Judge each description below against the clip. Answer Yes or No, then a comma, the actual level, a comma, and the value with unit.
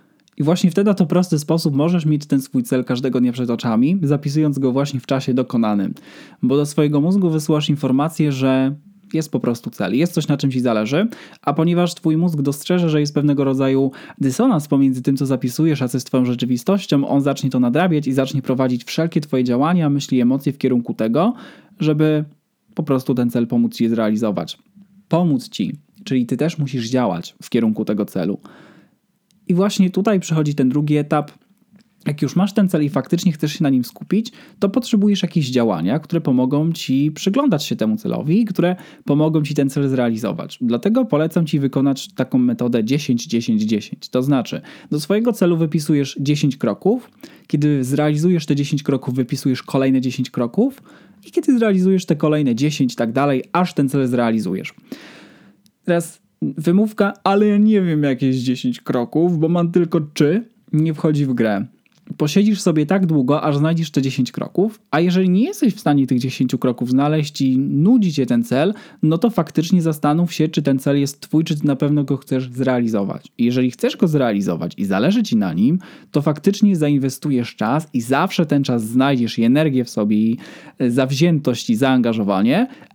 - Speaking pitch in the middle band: Yes, medium, 150 Hz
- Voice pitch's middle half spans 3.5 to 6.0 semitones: Yes, average, 5.2 semitones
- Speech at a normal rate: No, fast, 175 wpm